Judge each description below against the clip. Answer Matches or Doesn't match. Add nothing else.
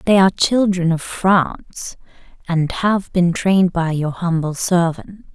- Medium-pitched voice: Matches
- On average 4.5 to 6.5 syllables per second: Doesn't match